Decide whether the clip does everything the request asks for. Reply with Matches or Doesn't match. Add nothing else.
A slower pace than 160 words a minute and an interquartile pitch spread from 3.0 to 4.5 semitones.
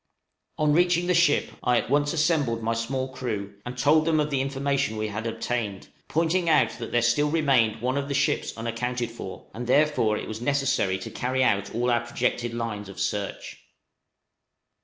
Doesn't match